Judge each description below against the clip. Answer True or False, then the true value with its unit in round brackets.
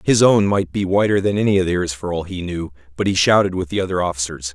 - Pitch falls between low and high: False (90 Hz)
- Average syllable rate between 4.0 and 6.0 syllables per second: False (6.2 syllables/s)